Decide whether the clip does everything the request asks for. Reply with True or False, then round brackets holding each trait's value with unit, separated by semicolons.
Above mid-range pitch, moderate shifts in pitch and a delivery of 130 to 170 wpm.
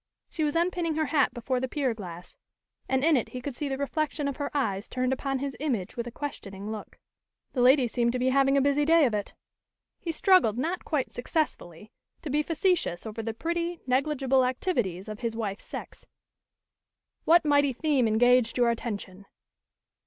False (260 Hz; 4.6 semitones; 185 wpm)